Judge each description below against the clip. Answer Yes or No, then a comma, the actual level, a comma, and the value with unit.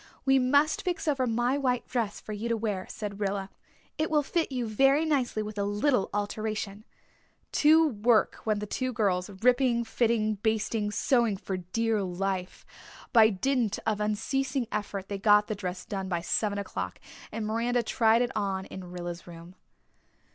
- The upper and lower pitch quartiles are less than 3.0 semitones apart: No, average, 3.6 semitones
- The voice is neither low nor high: No, high, 215 Hz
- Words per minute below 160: No, average, 170 wpm